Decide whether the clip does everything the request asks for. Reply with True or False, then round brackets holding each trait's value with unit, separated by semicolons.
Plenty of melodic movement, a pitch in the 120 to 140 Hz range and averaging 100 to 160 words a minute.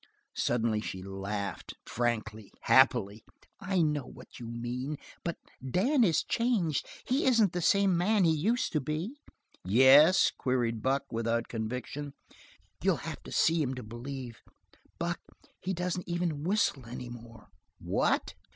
True (7.1 semitones; 135 Hz; 140 wpm)